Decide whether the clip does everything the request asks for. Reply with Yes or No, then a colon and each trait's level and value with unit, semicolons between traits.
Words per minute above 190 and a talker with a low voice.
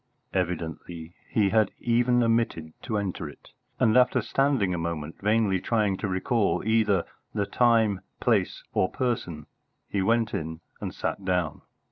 No: average, 145 wpm; low, 100 Hz